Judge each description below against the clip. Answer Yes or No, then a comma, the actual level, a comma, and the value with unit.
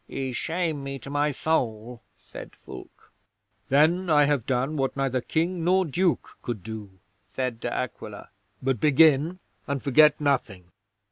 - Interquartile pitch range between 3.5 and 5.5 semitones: Yes, average, 4.0 semitones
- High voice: No, medium, 140 Hz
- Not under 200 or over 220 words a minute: No, average, 145 wpm